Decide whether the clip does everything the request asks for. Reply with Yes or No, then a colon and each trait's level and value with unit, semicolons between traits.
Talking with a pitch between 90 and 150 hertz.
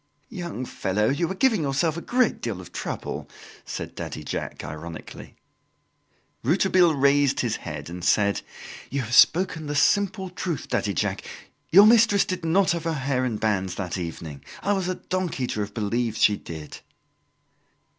Yes: medium, 140 Hz